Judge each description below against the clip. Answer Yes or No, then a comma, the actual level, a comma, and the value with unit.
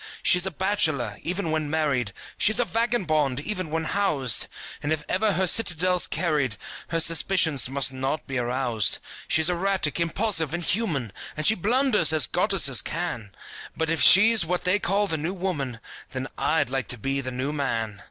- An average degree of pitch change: No, wide, 5.7 semitones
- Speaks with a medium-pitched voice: Yes, medium, 160 Hz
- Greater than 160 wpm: Yes, average, 170 wpm